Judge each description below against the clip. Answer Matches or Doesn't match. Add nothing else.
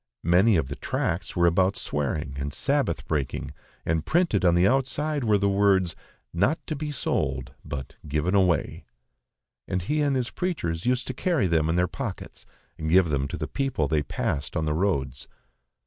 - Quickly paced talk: Doesn't match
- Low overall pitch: Matches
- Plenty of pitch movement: Matches